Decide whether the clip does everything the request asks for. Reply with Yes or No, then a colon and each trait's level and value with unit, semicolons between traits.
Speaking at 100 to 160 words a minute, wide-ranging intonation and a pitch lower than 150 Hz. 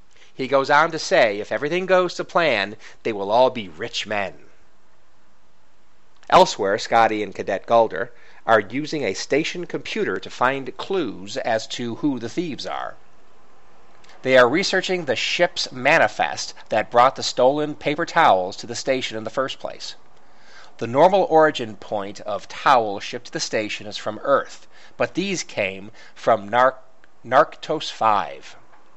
Yes: average, 155 wpm; wide, 6.0 semitones; low, 135 Hz